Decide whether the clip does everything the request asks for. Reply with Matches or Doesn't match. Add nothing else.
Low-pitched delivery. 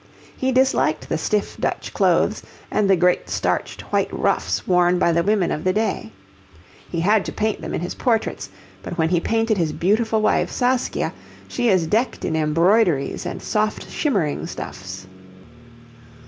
Doesn't match